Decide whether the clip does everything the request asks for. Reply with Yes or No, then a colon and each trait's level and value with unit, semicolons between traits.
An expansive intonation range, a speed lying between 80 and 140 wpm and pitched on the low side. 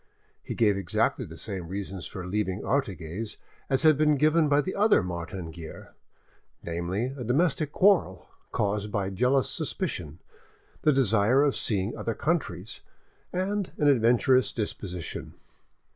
Yes: wide, 7.7 semitones; slow, 135 wpm; low, 115 Hz